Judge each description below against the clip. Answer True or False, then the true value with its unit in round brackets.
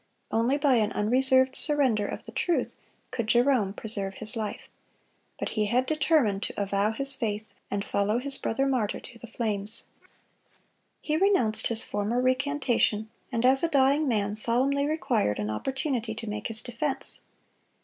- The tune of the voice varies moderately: True (4.2 semitones)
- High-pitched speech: True (235 Hz)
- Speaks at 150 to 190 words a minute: True (160 wpm)